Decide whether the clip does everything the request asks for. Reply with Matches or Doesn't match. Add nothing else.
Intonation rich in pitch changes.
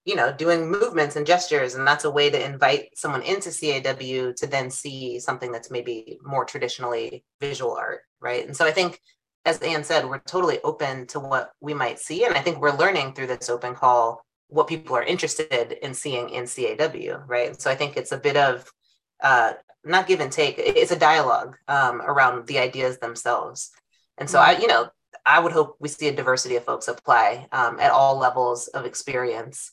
Matches